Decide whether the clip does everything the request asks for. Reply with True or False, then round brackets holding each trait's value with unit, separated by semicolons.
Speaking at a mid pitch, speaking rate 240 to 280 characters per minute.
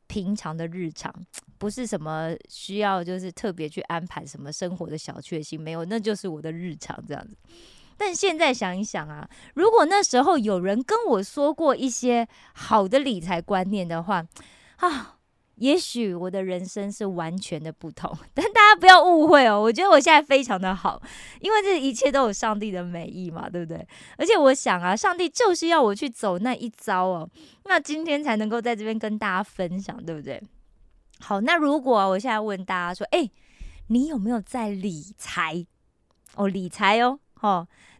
False (205 Hz; 275 characters per minute)